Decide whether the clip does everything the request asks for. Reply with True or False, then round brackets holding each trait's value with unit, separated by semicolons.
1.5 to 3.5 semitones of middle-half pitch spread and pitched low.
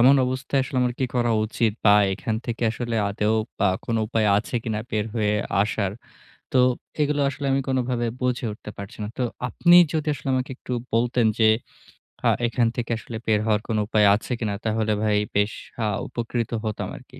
True (2.8 semitones; 115 Hz)